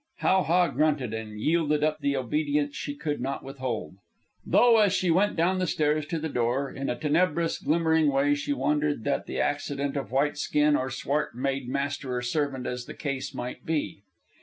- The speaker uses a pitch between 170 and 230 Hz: No, medium, 145 Hz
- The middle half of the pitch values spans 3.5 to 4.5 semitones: No, narrow, 2.6 semitones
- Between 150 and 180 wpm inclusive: No, average, 190 wpm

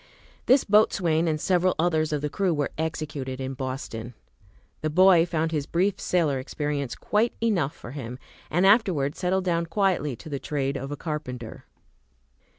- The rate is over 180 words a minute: No, average, 160 wpm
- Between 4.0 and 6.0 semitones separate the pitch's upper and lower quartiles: Yes, average, 4.6 semitones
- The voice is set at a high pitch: No, medium, 155 Hz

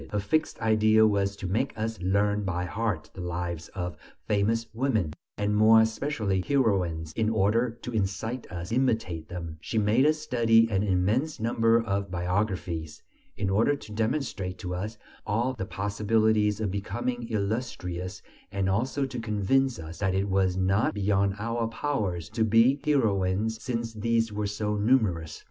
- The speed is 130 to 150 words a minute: No, average, 160 wpm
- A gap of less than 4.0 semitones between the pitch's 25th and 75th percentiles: Yes, average, 3.2 semitones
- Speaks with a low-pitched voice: Yes, low, 105 Hz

